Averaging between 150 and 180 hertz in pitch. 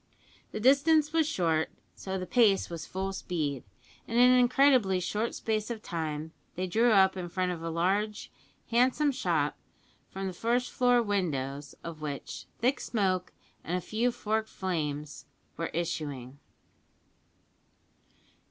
No: high, 190 Hz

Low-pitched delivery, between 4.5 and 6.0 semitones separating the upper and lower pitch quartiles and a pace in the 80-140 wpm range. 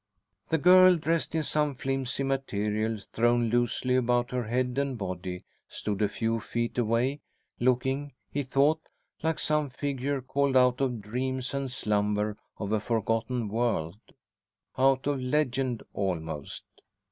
No: low, 125 Hz; average, 3.6 semitones; slow, 135 wpm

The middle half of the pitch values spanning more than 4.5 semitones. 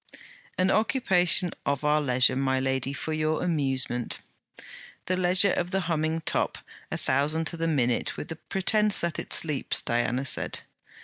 Yes: average, 5.0 semitones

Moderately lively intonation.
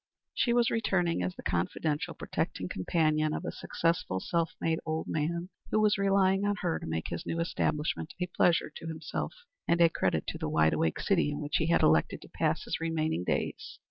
Yes: average, 3.3 semitones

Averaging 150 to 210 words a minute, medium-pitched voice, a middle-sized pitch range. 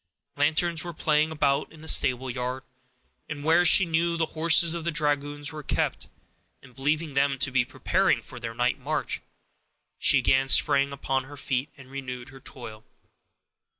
Yes: average, 165 wpm; medium, 145 Hz; average, 3.2 semitones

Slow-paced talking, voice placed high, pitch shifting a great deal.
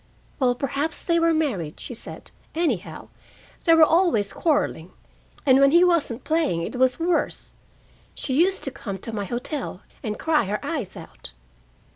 No: average, 160 wpm; very high, 275 Hz; wide, 6.7 semitones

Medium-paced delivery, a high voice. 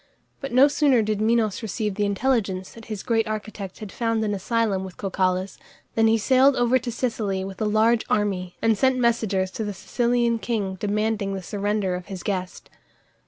Yes: average, 185 wpm; high, 215 Hz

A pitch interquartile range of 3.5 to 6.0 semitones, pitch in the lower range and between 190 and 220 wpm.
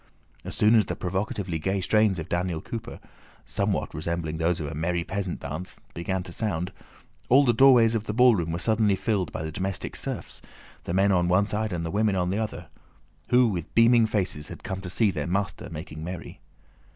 Yes: average, 4.0 semitones; very low, 95 Hz; average, 195 wpm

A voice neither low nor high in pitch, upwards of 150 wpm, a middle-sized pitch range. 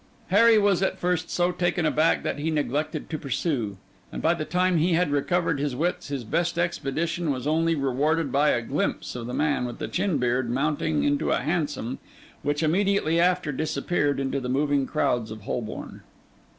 Yes: medium, 155 Hz; average, 185 wpm; average, 4.0 semitones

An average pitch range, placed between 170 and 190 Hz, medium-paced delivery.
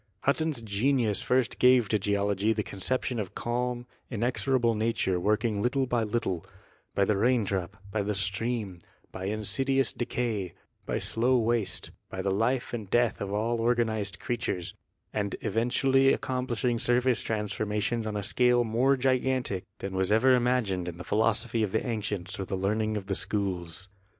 No: average, 3.5 semitones; low, 110 Hz; average, 165 wpm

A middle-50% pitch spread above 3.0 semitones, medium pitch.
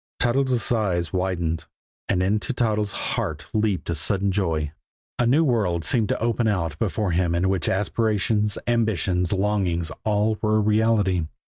No: average, 3.8 semitones; low, 100 Hz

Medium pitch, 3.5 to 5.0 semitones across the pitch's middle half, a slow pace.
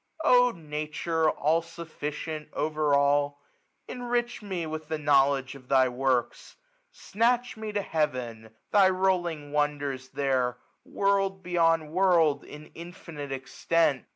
Yes: medium, 155 Hz; average, 4.2 semitones; slow, 125 wpm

